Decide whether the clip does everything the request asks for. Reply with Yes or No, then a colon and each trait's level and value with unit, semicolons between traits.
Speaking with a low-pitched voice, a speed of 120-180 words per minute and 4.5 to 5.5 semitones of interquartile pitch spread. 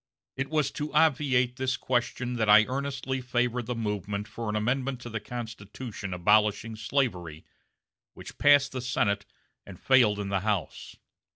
No: low, 120 Hz; average, 155 wpm; average, 3.9 semitones